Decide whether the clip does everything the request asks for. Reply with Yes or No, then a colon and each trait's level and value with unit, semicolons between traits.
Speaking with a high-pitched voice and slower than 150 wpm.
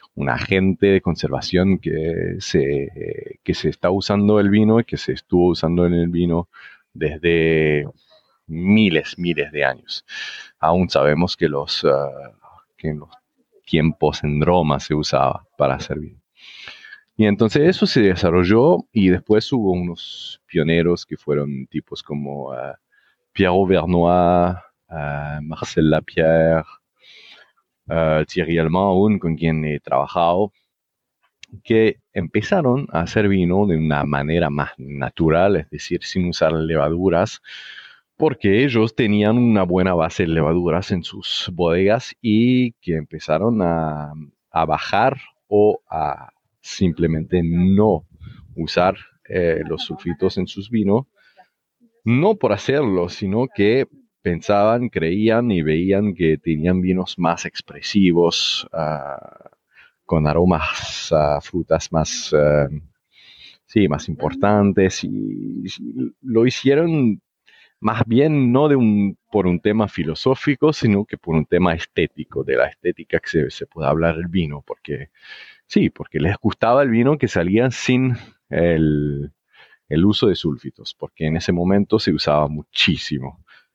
No: very low, 90 Hz; average, 130 wpm